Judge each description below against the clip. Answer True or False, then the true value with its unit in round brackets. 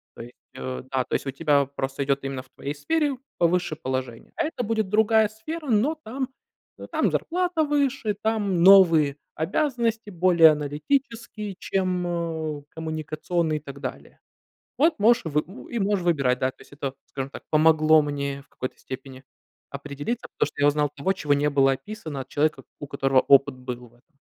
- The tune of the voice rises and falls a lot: True (7.4 semitones)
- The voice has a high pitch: False (155 Hz)